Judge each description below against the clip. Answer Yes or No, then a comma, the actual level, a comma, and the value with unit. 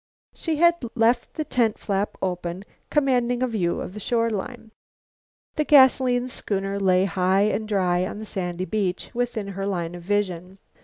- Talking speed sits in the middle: Yes, average, 165 wpm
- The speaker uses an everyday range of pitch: Yes, average, 4.7 semitones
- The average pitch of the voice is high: Yes, high, 205 Hz